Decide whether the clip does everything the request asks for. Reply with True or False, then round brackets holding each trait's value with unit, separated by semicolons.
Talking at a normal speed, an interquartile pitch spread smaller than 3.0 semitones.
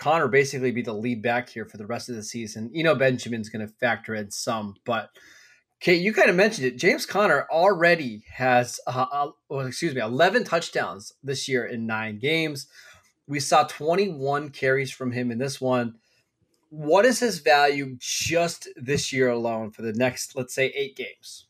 False (195 wpm; 3.8 semitones)